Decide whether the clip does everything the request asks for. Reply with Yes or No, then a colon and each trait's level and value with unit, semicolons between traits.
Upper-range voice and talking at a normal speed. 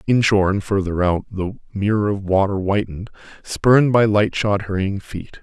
No: low, 100 Hz; average, 155 wpm